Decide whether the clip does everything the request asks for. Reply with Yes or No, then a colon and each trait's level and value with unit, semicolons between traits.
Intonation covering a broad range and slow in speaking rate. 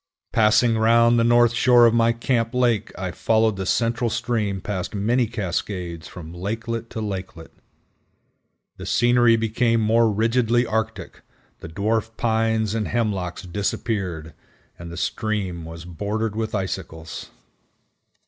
No: average, 3.4 semitones; slow, 130 wpm